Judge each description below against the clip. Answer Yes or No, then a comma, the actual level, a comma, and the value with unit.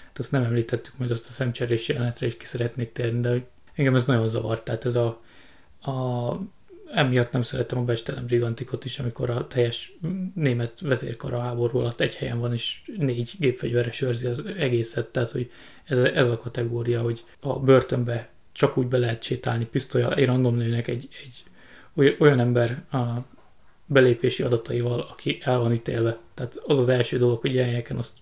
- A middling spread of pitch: No, narrow, 1.5 semitones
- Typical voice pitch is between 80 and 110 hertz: No, low, 120 Hz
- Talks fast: Yes, fast, 175 wpm